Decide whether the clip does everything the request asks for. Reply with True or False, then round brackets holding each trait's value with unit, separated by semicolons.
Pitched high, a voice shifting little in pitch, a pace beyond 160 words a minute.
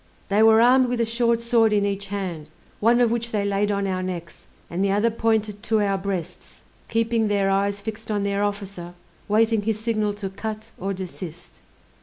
True (205 Hz; 2.2 semitones; 195 wpm)